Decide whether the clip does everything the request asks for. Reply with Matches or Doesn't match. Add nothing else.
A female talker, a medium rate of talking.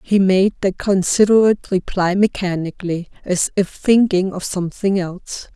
Doesn't match